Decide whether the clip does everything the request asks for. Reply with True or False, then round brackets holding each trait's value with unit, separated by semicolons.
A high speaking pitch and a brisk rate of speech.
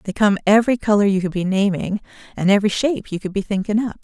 True (205 Hz; 240 wpm)